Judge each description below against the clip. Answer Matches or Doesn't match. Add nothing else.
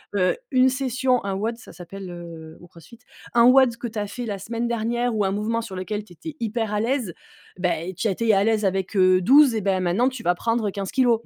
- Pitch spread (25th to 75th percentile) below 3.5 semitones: Doesn't match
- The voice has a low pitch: Doesn't match